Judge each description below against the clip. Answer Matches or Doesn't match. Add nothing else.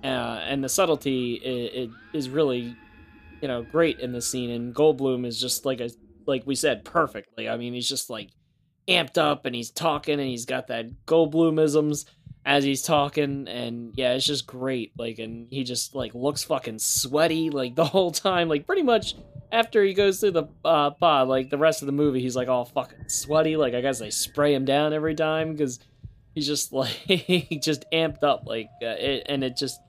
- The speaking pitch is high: Doesn't match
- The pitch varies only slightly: Doesn't match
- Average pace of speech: Doesn't match